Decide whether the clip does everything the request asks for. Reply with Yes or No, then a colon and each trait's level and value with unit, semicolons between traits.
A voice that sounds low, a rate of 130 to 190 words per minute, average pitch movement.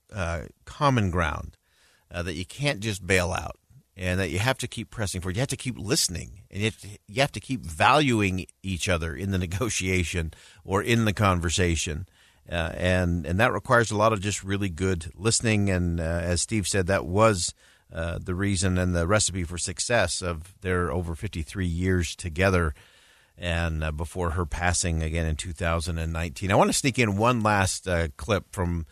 No: very low, 95 Hz; average, 200 wpm; average, 3.3 semitones